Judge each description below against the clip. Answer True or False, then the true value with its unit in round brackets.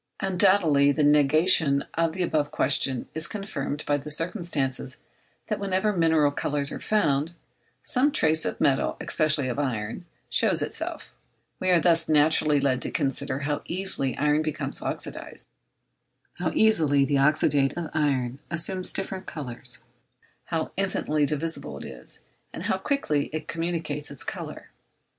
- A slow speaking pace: False (145 wpm)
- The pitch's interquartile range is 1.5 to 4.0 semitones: True (3.4 semitones)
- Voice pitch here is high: False (150 Hz)